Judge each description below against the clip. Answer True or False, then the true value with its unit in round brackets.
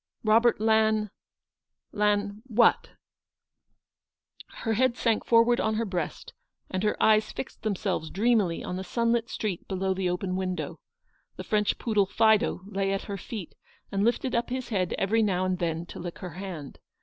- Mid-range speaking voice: False (210 Hz)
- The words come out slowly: False (175 wpm)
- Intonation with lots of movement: False (3.2 semitones)